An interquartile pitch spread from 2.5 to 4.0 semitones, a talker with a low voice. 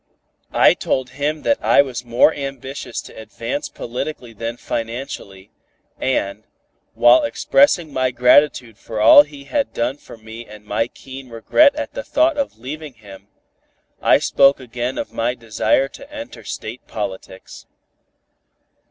No: average, 4.6 semitones; low, 125 Hz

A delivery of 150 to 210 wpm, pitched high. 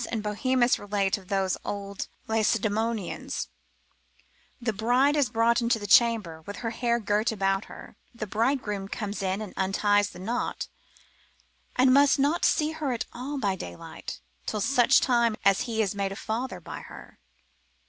Yes: average, 160 wpm; high, 220 Hz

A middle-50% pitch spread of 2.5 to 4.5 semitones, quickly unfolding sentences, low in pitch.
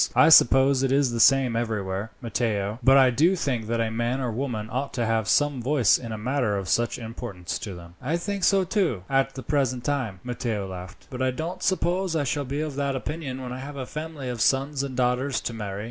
Yes: average, 3.9 semitones; fast, 235 wpm; low, 130 Hz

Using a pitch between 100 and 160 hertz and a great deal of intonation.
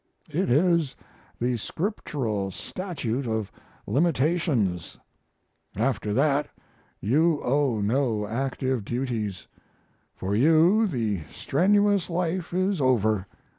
Yes: low, 135 Hz; wide, 7.3 semitones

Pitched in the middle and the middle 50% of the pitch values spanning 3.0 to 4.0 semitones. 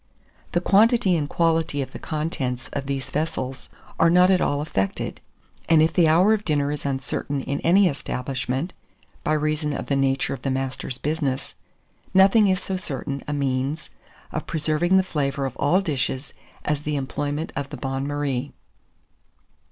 Yes: medium, 145 Hz; average, 3.4 semitones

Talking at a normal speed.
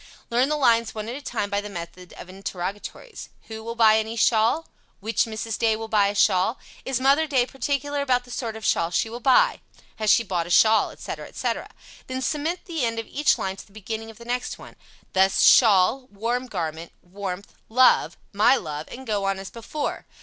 No: fast, 210 wpm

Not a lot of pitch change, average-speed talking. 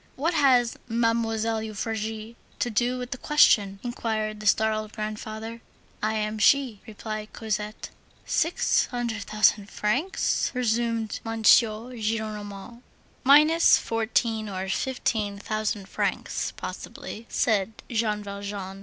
No: narrow, 1.8 semitones; slow, 110 wpm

